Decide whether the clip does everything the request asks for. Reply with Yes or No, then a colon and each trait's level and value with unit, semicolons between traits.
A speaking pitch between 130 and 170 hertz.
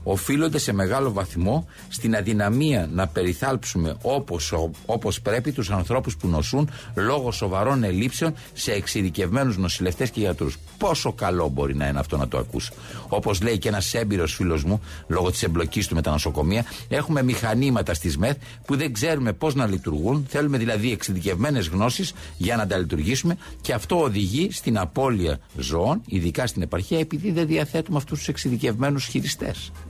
No: low, 105 Hz